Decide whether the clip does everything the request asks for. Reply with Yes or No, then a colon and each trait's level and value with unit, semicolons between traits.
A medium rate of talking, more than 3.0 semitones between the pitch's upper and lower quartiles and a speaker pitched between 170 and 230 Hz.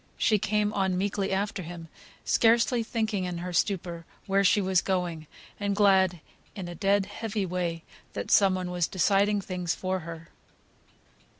No: average, 160 wpm; narrow, 2.4 semitones; high, 190 Hz